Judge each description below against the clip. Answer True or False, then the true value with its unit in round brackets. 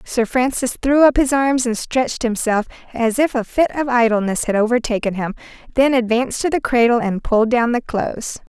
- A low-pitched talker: False (240 Hz)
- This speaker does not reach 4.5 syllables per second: False (5.4 syllables/s)